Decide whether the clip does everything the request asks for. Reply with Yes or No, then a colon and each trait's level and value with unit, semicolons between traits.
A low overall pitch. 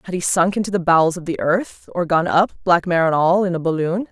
No: medium, 175 Hz